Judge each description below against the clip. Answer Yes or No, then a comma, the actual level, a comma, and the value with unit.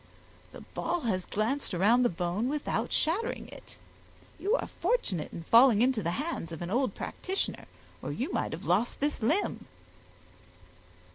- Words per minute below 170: Yes, average, 155 wpm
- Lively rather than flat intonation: Yes, wide, 8.2 semitones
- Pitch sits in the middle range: No, high, 240 Hz